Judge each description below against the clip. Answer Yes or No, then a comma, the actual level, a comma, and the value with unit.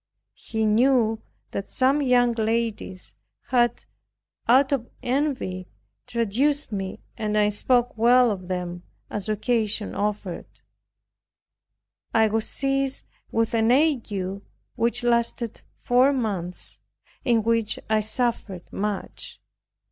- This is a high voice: Yes, high, 225 Hz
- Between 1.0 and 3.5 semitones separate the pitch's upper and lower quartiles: Yes, average, 2.9 semitones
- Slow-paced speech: Yes, slow, 110 wpm